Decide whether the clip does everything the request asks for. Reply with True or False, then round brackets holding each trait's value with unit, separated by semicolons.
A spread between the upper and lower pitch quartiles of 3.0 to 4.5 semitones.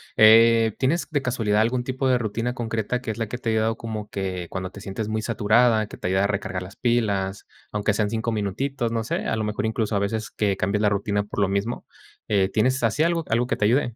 False (2.6 semitones)